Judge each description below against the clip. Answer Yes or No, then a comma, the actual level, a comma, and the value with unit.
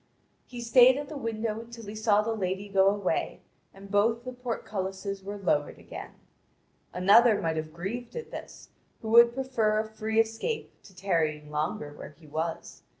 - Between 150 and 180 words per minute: Yes, average, 170 wpm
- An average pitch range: Yes, average, 3.6 semitones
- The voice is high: Yes, high, 210 Hz